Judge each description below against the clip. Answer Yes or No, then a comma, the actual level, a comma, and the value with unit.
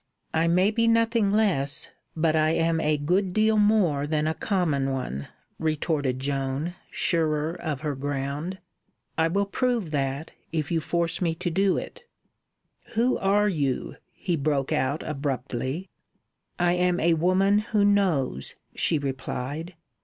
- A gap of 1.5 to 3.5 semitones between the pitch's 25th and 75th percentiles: No, average, 5.0 semitones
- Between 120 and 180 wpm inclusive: Yes, average, 145 wpm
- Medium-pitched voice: Yes, medium, 160 Hz